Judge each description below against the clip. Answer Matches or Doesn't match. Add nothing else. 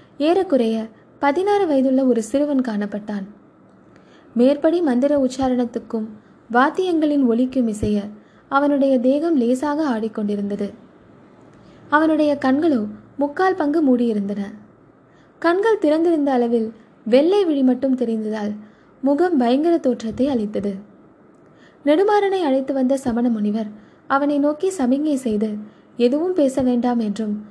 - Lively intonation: Doesn't match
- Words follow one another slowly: Doesn't match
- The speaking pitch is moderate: Doesn't match